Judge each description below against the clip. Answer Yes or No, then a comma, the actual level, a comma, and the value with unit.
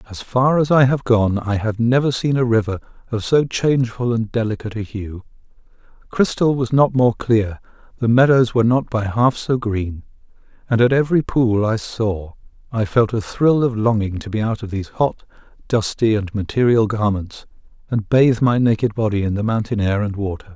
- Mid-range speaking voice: No, low, 115 Hz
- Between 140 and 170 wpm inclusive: No, average, 190 wpm